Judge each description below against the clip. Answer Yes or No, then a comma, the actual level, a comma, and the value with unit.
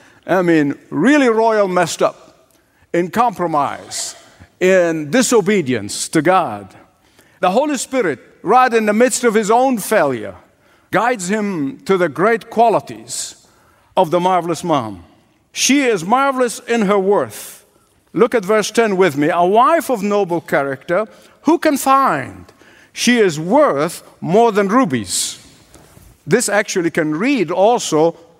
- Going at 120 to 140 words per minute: Yes, slow, 135 wpm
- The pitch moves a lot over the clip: Yes, wide, 6.0 semitones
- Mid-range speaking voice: No, high, 215 Hz